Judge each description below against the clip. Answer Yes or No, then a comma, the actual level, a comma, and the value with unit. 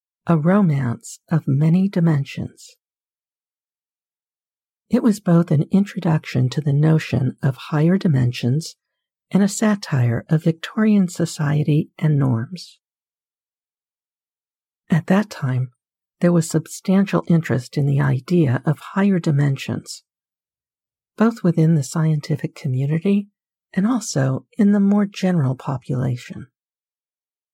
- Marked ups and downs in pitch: Yes, wide, 6.4 semitones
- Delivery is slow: Yes, slow, 105 wpm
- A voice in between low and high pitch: Yes, medium, 155 Hz